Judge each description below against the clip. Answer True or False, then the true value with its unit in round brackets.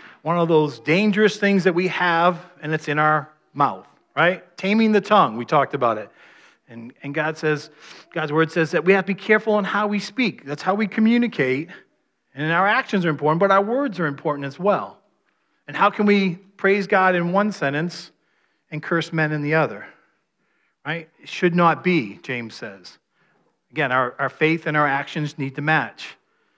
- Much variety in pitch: False (4.4 semitones)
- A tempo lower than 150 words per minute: False (195 wpm)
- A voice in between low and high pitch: True (165 Hz)